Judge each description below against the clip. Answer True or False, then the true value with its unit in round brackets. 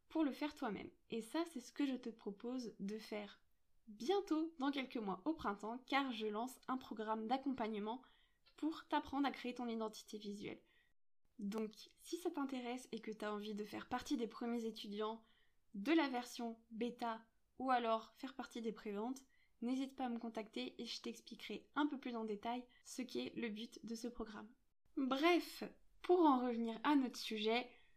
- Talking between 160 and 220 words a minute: True (180 wpm)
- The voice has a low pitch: False (240 Hz)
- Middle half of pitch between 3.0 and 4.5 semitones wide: True (3.5 semitones)